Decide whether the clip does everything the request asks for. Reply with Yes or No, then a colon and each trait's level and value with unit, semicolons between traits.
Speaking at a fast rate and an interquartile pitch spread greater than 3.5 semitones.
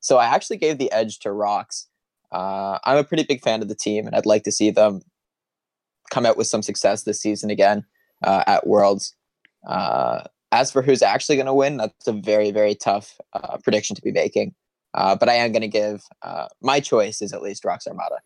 No: fast, 220 wpm; narrow, 2.4 semitones